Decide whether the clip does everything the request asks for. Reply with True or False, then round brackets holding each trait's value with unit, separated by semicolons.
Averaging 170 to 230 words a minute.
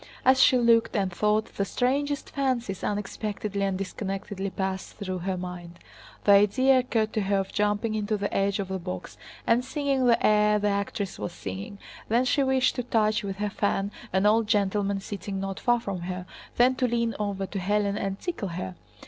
True (190 wpm)